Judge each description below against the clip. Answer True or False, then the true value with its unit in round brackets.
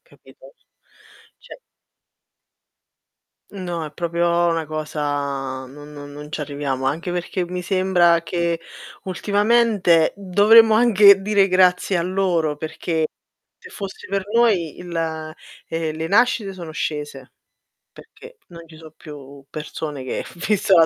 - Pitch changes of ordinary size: True (4.0 semitones)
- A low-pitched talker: False (170 Hz)